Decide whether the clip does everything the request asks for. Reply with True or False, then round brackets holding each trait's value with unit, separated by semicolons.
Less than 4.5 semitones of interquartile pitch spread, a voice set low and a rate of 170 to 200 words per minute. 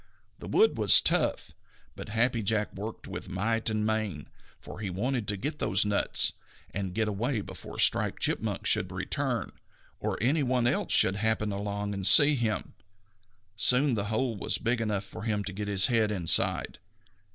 True (2.5 semitones; 105 Hz; 175 wpm)